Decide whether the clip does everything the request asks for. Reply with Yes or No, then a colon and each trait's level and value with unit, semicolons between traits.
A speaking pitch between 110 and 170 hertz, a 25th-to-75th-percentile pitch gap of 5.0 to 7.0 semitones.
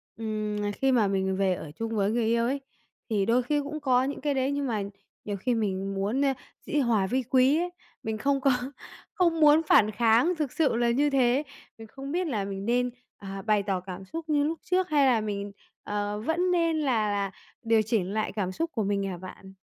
No: high, 230 Hz; wide, 5.5 semitones